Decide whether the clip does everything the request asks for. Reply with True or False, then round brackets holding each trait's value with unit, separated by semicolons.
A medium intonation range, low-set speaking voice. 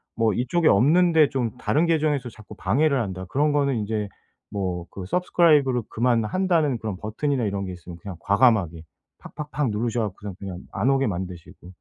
False (6.7 semitones; 115 Hz)